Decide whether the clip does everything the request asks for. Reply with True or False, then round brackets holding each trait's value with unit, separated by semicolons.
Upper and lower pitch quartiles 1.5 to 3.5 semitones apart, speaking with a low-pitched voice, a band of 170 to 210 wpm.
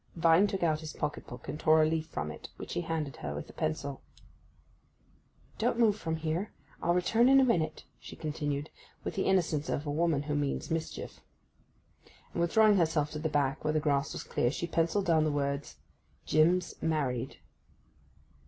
False (2.8 semitones; 155 Hz; 180 wpm)